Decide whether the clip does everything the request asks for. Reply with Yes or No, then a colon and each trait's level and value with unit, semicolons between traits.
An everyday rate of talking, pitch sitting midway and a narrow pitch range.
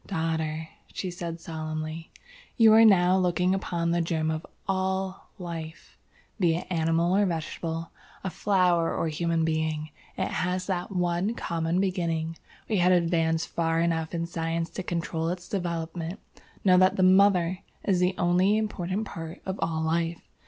Yes: average, 160 wpm; medium, 170 Hz; narrow, 2.2 semitones